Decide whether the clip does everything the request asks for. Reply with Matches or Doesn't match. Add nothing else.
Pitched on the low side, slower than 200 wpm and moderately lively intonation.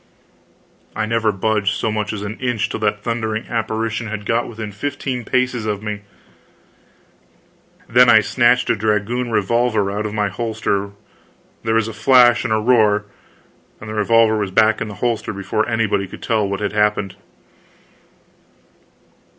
Doesn't match